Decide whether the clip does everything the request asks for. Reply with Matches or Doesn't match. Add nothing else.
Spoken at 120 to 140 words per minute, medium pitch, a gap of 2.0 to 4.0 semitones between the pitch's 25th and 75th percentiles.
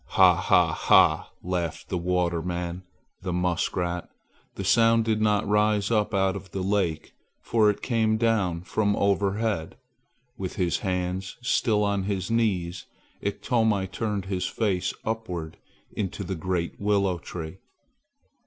Doesn't match